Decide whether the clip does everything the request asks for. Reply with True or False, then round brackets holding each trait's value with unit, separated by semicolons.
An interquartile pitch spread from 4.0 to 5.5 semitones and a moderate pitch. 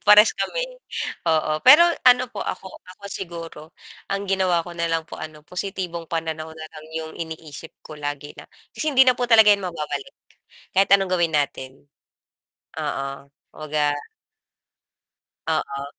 True (4.3 semitones; 165 Hz)